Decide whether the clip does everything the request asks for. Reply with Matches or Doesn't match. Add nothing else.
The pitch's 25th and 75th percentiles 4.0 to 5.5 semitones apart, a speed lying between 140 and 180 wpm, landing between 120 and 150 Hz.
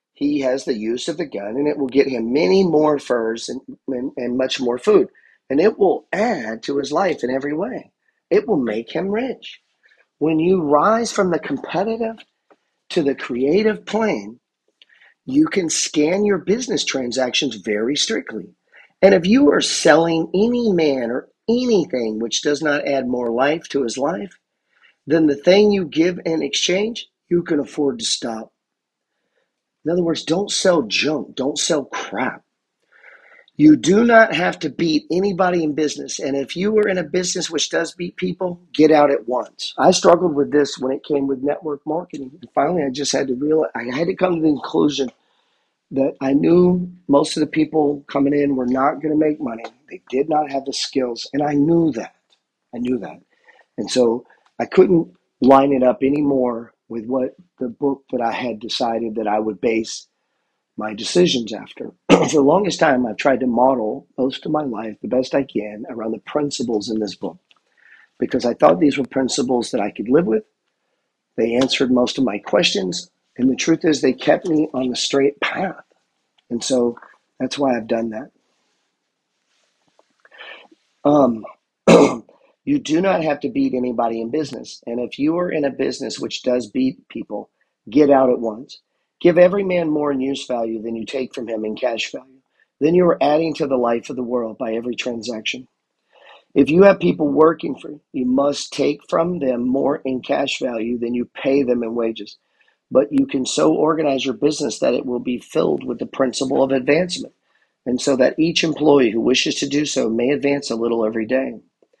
Doesn't match